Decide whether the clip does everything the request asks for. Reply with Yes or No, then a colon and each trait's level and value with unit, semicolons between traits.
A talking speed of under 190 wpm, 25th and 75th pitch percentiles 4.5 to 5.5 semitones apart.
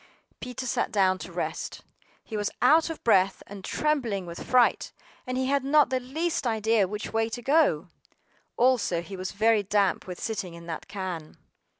Yes: average, 180 wpm; average, 5.1 semitones